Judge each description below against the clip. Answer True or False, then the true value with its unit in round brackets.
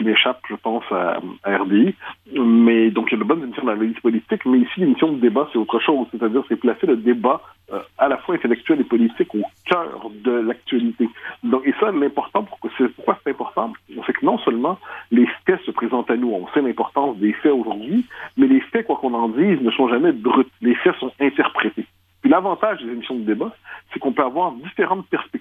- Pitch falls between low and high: False (125 Hz)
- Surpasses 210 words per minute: True (220 wpm)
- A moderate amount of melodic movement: False (7.6 semitones)